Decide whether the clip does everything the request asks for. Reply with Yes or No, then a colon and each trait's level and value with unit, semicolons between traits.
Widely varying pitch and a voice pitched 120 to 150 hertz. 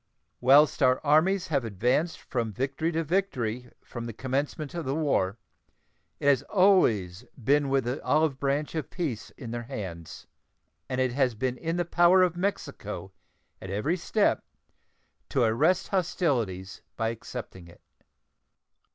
Yes: wide, 5.8 semitones; low, 135 Hz